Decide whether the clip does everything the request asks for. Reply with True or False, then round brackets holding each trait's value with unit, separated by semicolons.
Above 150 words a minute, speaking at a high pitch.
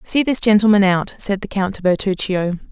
True (200 wpm; 200 Hz)